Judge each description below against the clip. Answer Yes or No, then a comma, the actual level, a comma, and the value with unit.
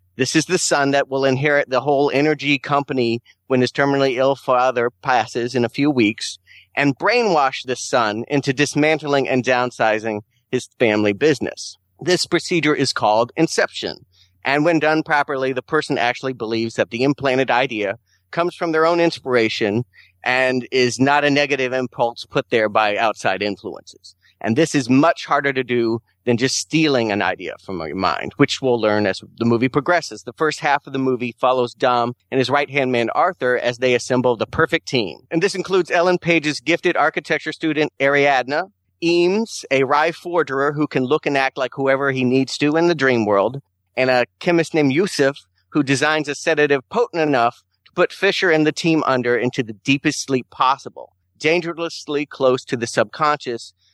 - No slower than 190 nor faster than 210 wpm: No, average, 180 wpm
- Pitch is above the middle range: No, low, 135 Hz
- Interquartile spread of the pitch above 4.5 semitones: No, average, 3.9 semitones